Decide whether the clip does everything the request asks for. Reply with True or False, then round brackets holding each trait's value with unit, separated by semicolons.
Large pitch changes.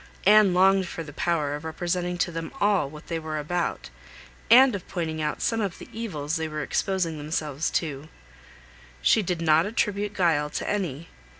False (4.0 semitones)